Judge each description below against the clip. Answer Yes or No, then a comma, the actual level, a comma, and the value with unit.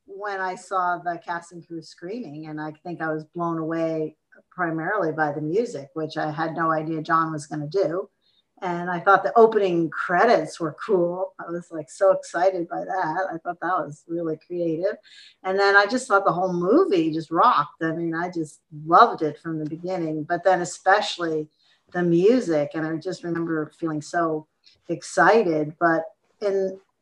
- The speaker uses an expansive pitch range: No, average, 2.9 semitones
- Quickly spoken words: No, average, 180 wpm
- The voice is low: No, medium, 170 Hz